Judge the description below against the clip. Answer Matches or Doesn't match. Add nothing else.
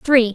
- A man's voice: Doesn't match